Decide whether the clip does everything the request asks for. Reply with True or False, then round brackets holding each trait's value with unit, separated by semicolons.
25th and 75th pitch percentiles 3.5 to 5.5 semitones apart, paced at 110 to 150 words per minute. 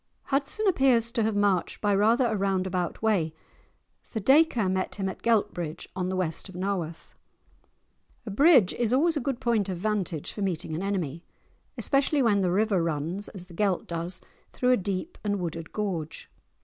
False (4.4 semitones; 180 wpm)